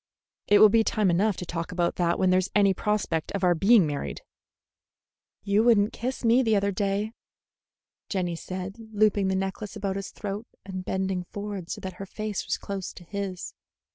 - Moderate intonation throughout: No, narrow, 2.3 semitones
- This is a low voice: No, high, 195 Hz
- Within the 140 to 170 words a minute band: No, average, 190 wpm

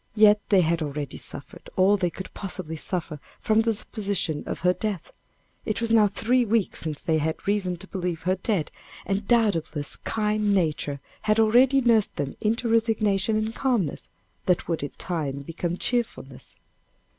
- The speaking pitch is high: Yes, high, 195 Hz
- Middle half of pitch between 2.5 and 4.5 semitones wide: No, average, 4.9 semitones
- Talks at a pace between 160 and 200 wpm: Yes, average, 165 wpm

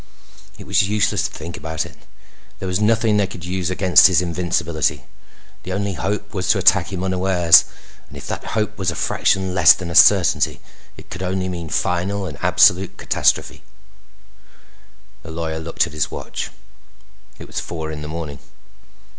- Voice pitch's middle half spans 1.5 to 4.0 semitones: Yes, narrow, 2.5 semitones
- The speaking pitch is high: No, very low, 90 Hz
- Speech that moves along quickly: No, average, 170 wpm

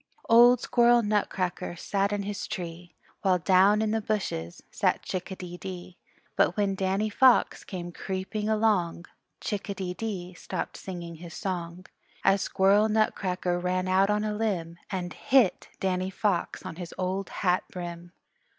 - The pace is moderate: Yes, average, 160 wpm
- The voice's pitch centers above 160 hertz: Yes, high, 190 Hz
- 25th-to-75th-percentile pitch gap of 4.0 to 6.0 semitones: No, average, 2.8 semitones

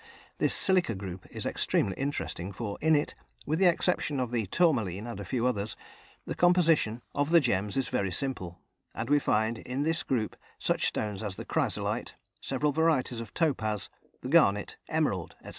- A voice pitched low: Yes, low, 125 Hz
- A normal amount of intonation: No, wide, 6.8 semitones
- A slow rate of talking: No, average, 175 wpm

